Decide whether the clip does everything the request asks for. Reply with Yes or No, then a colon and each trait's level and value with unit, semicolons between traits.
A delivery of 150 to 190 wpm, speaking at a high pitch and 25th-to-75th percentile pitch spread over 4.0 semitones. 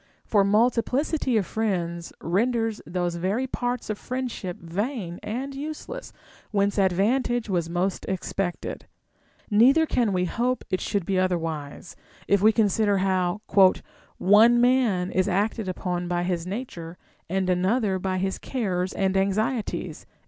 No: average, 140 wpm; high, 200 Hz; average, 4.5 semitones